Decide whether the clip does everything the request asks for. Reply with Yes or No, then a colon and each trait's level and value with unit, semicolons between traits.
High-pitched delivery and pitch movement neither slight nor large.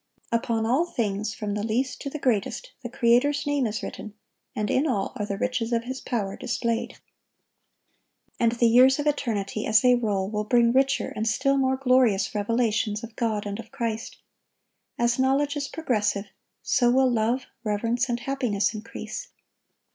Yes: high, 235 Hz; average, 3.4 semitones